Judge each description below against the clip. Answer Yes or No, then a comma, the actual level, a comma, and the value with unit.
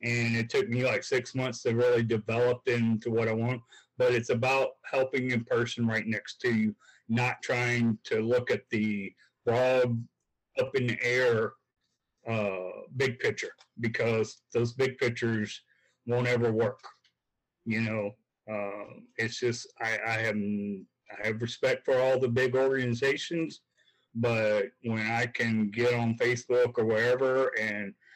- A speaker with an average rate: Yes, average, 150 wpm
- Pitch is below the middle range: Yes, low, 115 Hz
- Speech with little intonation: Yes, narrow, 1.8 semitones